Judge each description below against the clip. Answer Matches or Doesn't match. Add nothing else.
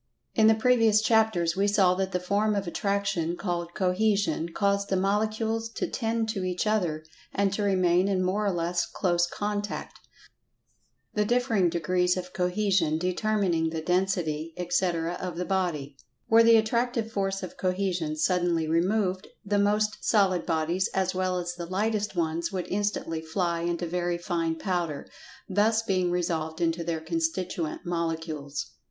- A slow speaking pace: Doesn't match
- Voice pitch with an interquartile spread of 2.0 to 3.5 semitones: Matches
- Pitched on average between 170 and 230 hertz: Matches